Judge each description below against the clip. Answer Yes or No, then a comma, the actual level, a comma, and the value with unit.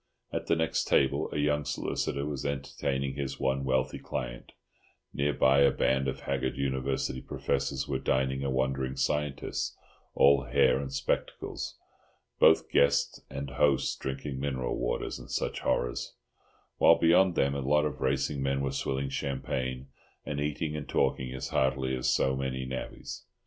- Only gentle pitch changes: Yes, narrow, 1.2 semitones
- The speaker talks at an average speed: Yes, average, 155 wpm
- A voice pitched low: Yes, very low, 70 Hz